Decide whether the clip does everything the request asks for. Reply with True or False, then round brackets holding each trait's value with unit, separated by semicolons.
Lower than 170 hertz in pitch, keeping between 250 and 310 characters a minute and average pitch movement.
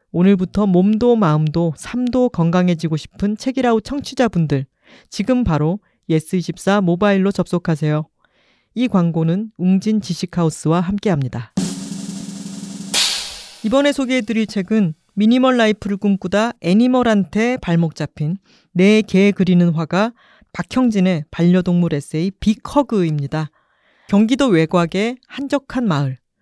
False (195 Hz; 280 characters per minute; 4.6 semitones)